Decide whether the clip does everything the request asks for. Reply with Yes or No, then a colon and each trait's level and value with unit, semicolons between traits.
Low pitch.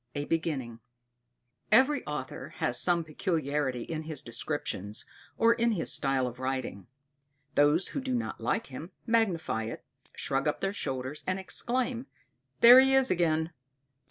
No: medium, 160 Hz